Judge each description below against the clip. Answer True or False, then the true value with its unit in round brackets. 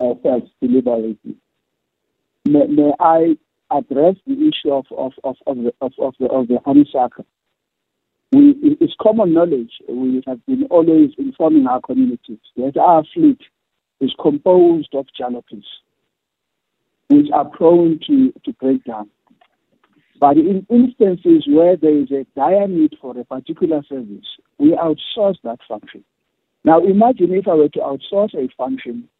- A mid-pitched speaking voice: True (155 Hz)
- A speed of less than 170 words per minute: True (140 wpm)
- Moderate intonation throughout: False (6.5 semitones)